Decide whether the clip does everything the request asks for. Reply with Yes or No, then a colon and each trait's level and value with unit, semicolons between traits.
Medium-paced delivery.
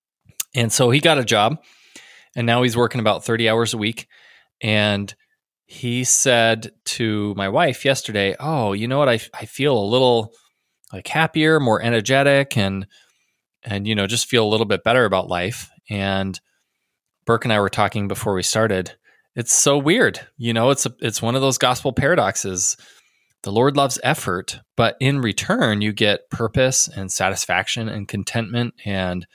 Yes: average, 170 wpm